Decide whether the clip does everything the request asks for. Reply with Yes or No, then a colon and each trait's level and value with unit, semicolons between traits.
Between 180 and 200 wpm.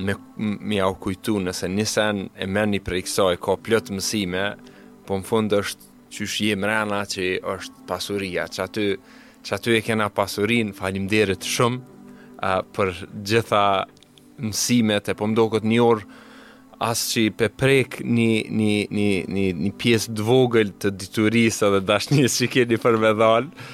No: average, 155 wpm